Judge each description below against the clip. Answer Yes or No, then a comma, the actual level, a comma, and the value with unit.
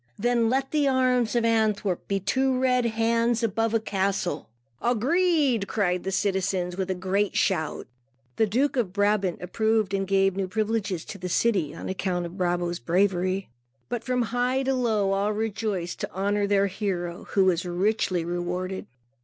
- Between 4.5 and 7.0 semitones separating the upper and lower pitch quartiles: No, average, 3.7 semitones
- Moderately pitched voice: No, high, 200 Hz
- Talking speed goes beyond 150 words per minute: Yes, average, 165 wpm